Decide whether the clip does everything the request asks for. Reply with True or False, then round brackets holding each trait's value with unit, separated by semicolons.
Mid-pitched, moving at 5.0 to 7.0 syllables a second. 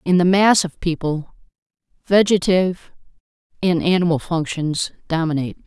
True (170 Hz; 5.3 syllables/s)